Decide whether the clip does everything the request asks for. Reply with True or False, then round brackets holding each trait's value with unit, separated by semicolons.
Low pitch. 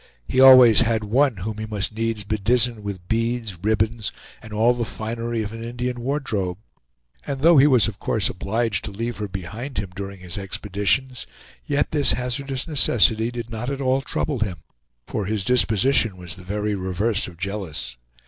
True (110 Hz)